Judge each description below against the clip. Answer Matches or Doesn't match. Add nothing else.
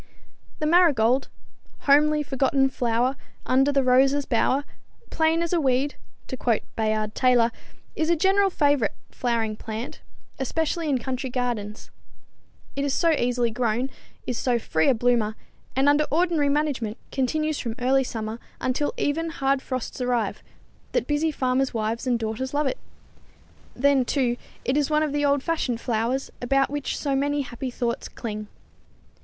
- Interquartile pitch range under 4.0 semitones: Matches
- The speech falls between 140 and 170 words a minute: Matches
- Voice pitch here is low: Doesn't match